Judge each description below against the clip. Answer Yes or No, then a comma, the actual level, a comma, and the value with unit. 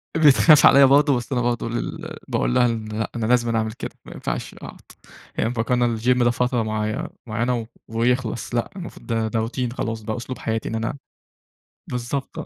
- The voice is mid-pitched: No, low, 120 Hz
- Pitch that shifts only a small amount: Yes, narrow, 1.8 semitones